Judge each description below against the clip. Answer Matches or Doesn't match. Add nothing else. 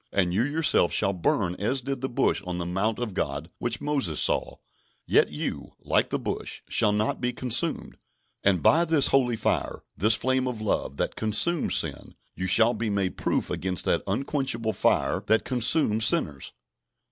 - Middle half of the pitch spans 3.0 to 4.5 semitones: Doesn't match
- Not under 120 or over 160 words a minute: Doesn't match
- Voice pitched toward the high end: Doesn't match